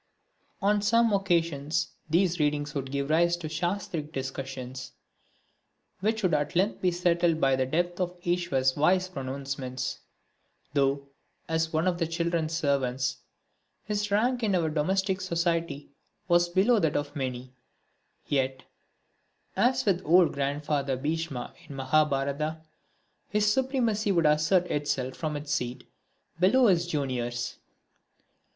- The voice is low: No, medium, 160 Hz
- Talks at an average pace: No, slow, 130 wpm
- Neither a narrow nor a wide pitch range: Yes, average, 4.7 semitones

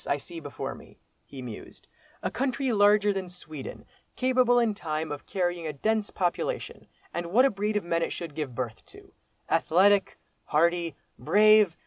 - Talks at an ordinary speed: Yes, average, 165 wpm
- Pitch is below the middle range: No, medium, 180 Hz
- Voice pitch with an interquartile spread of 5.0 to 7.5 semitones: Yes, average, 5.3 semitones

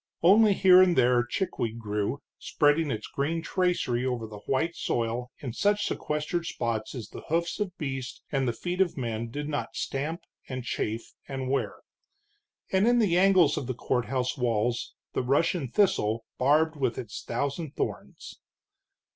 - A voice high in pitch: No, low, 135 Hz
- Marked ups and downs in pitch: Yes, wide, 5.9 semitones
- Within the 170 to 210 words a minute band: No, average, 160 wpm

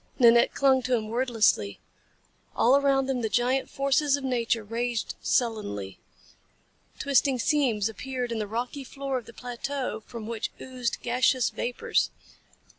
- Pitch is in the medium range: No, high, 245 Hz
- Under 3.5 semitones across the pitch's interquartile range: Yes, average, 2.7 semitones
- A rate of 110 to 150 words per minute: Yes, average, 140 wpm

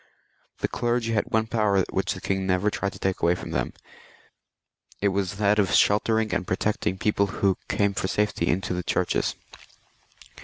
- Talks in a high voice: No, low, 100 Hz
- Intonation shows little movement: Yes, narrow, 2.0 semitones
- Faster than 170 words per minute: No, average, 165 wpm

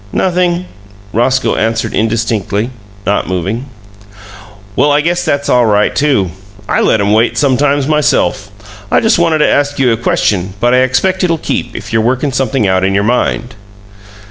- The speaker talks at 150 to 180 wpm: Yes, average, 170 wpm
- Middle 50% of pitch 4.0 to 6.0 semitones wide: Yes, average, 5.1 semitones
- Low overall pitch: Yes, low, 125 Hz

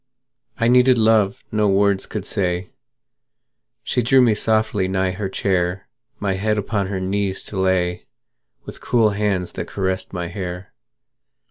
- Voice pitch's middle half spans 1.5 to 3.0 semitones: Yes, narrow, 2.4 semitones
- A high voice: No, low, 100 Hz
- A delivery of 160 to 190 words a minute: No, average, 145 wpm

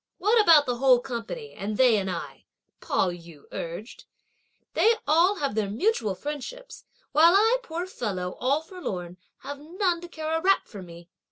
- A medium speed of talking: Yes, average, 170 wpm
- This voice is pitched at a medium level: No, very high, 285 Hz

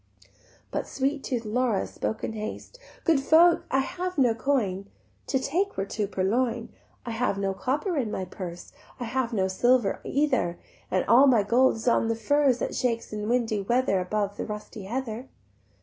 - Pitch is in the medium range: No, high, 235 Hz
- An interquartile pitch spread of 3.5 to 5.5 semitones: Yes, average, 4.1 semitones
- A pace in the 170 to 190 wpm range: Yes, average, 180 wpm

